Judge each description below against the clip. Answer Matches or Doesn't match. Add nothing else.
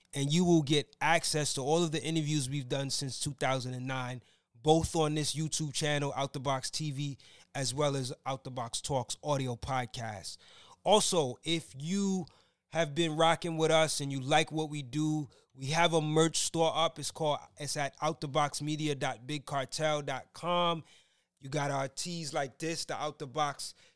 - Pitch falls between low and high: Matches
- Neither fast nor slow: Matches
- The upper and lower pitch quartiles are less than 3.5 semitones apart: Matches